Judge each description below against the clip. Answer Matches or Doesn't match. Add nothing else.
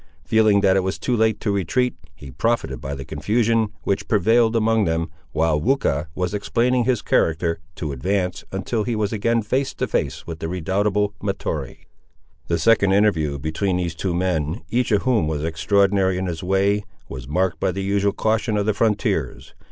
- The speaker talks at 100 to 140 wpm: Doesn't match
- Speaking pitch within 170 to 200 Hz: Doesn't match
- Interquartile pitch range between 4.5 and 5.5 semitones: Matches